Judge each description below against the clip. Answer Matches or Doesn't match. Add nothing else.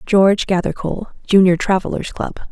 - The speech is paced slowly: Matches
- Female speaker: Matches